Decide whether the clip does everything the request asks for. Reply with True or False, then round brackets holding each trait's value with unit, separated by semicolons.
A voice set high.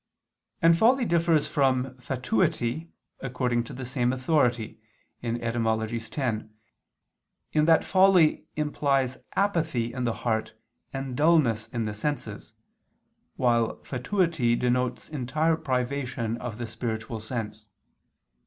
False (125 Hz)